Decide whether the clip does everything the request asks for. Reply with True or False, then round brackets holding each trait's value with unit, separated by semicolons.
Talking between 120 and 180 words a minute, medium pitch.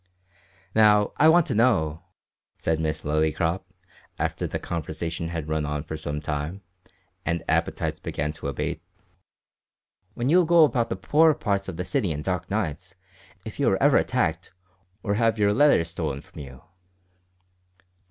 False (155 wpm; 85 Hz)